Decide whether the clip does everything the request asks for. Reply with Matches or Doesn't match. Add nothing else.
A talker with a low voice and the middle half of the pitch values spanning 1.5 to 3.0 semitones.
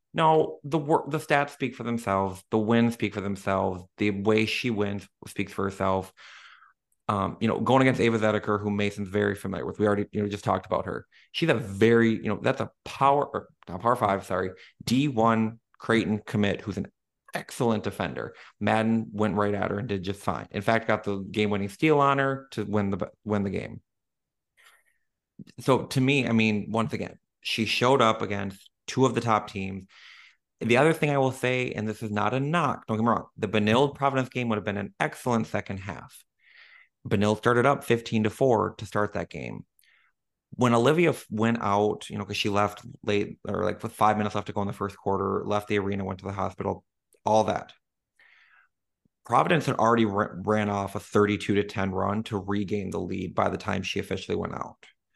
Matches